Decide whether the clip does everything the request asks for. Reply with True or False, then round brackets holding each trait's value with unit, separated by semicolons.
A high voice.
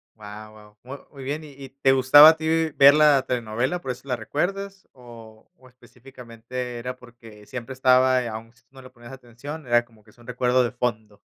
False (125 Hz)